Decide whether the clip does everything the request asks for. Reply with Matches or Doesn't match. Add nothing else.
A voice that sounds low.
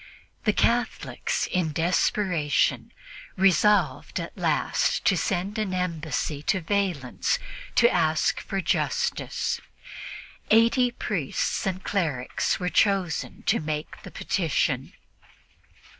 Doesn't match